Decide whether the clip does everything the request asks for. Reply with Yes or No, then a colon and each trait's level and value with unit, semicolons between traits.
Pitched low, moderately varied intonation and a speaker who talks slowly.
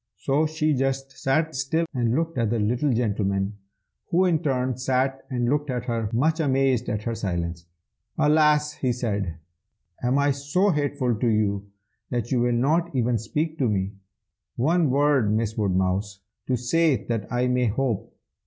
No: low, 125 Hz; average, 4.6 semitones; average, 165 wpm